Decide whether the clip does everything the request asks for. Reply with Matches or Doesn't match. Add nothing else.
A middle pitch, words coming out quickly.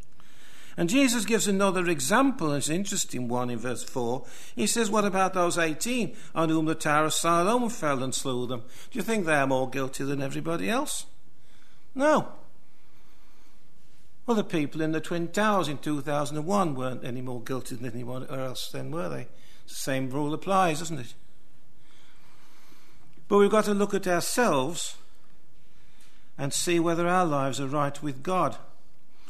Doesn't match